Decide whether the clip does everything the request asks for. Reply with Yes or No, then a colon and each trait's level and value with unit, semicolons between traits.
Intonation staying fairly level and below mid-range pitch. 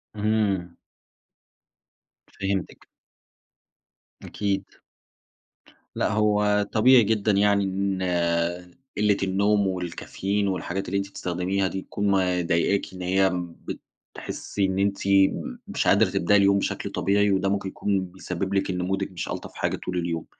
Yes: narrow, 1.6 semitones; very low, 95 Hz